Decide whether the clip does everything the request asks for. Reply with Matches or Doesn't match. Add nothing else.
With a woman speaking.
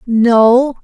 Matches